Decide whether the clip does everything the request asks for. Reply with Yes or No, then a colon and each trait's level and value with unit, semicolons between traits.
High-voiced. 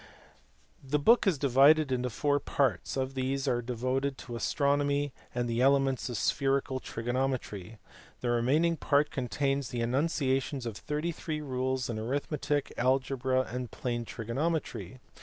No: low, 130 Hz